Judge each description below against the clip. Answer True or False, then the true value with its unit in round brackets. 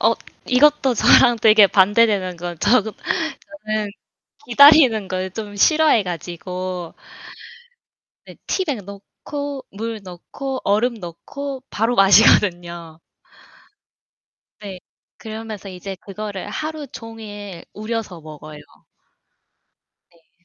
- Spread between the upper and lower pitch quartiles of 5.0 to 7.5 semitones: False (4.6 semitones)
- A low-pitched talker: False (210 Hz)